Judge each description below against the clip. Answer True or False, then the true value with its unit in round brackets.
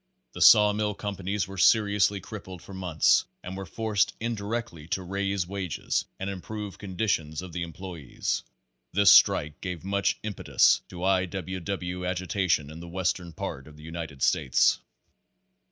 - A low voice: True (95 Hz)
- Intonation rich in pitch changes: False (2.7 semitones)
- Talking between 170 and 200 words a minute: False (155 wpm)